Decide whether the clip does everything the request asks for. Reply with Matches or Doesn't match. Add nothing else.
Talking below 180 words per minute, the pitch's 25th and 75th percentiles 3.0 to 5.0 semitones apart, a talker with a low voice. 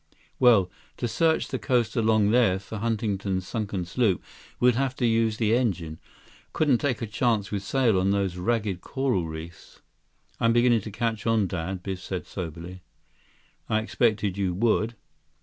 Matches